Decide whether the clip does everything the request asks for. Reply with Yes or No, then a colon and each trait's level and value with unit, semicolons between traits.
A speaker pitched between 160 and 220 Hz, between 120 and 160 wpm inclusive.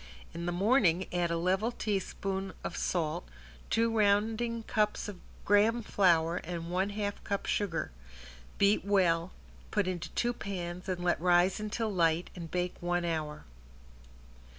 Yes: medium, 185 Hz; average, 145 wpm